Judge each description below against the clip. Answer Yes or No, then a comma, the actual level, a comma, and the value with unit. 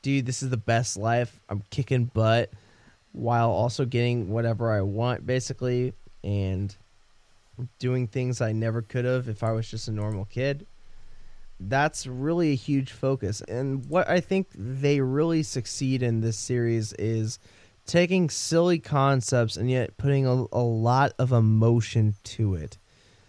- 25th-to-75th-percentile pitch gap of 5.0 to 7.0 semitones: No, average, 3.4 semitones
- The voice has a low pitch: Yes, low, 120 Hz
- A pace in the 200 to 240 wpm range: No, average, 150 wpm